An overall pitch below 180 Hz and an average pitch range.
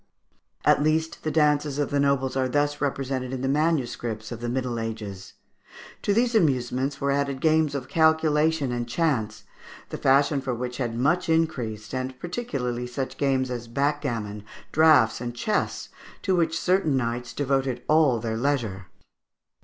Yes: low, 135 Hz; average, 3.9 semitones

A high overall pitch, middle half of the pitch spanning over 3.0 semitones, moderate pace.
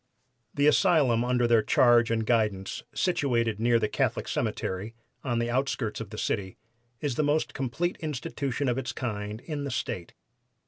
No: low, 120 Hz; average, 4.0 semitones; average, 165 wpm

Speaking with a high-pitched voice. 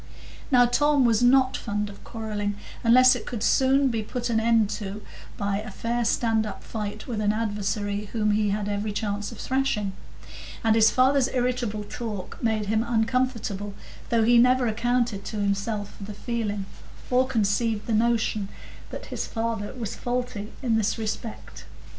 Yes: high, 220 Hz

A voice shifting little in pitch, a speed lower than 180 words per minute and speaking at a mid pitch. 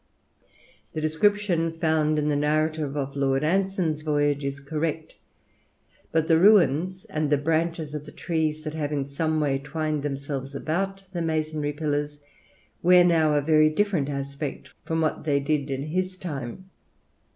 Yes: narrow, 2.0 semitones; average, 155 wpm; medium, 155 Hz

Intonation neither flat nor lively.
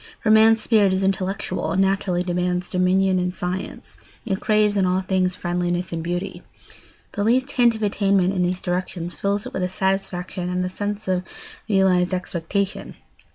No: narrow, 1.8 semitones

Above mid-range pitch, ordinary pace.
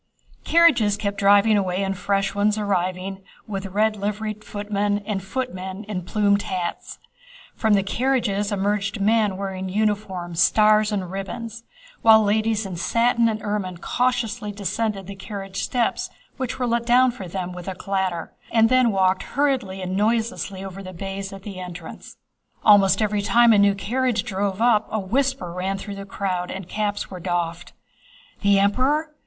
Yes: high, 205 Hz; average, 160 wpm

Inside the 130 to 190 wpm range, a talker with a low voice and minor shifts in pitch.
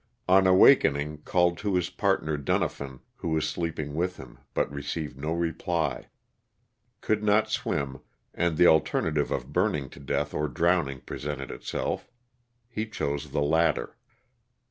No: average, 140 wpm; very low, 80 Hz; average, 3.6 semitones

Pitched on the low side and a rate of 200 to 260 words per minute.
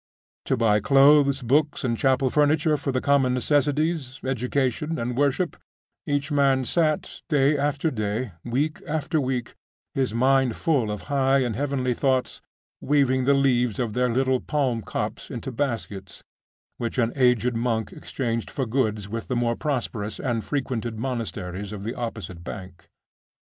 No: low, 130 Hz; average, 150 wpm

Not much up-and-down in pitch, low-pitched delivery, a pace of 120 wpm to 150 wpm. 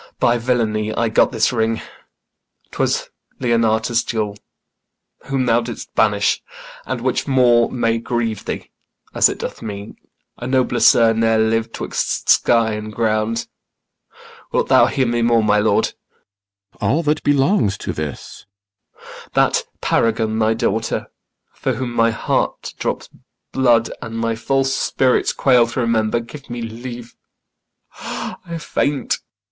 Yes: narrow, 1.9 semitones; low, 115 Hz; slow, 135 wpm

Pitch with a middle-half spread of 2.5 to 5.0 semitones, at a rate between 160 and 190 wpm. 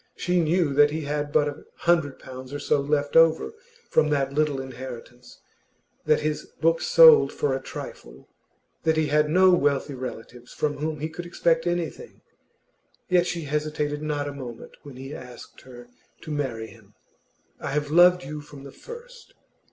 Yes: average, 2.9 semitones; average, 170 wpm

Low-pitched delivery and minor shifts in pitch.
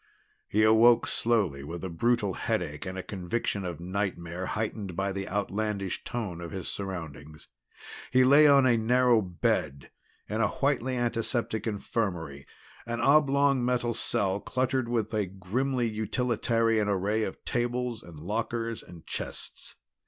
No: low, 110 Hz; average, 4.3 semitones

